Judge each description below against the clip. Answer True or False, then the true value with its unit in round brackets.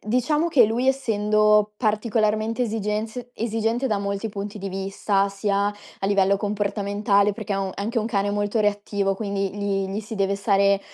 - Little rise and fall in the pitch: True (1.8 semitones)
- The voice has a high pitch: True (205 Hz)